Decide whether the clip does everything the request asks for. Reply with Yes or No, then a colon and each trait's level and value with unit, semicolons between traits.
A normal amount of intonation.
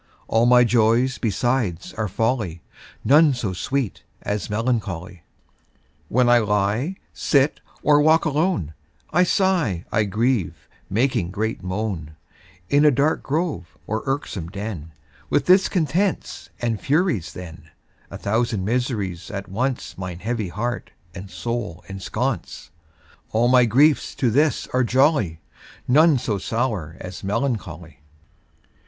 No: wide, 5.9 semitones